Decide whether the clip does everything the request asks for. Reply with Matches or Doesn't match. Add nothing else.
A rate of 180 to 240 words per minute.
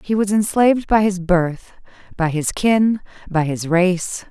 Doesn't match